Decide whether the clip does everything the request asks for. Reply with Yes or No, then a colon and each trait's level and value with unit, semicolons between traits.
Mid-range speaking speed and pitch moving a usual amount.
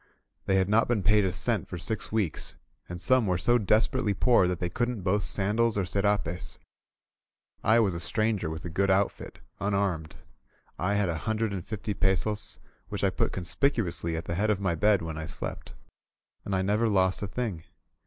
Yes: average, 195 wpm; average, 3.3 semitones